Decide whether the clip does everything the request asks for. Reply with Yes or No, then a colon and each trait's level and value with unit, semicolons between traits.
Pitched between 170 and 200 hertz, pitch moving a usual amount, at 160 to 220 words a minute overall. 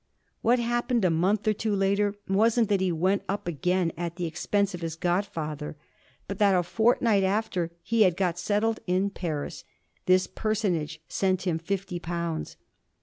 Yes: high, 190 Hz; average, 3.3 semitones; average, 165 wpm